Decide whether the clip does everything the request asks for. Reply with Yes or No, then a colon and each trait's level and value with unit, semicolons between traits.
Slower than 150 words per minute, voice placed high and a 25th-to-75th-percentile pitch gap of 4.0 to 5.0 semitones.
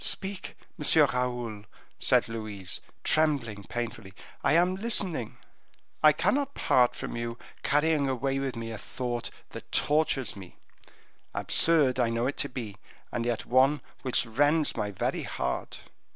No: average, 140 wpm; low, 125 Hz; average, 4.6 semitones